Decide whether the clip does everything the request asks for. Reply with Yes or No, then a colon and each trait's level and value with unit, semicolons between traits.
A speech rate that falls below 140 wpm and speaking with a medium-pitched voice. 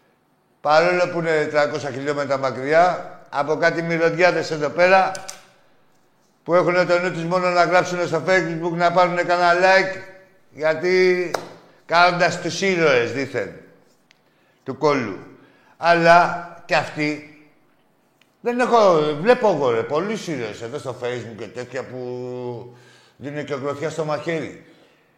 Yes: average, 125 wpm; medium, 165 Hz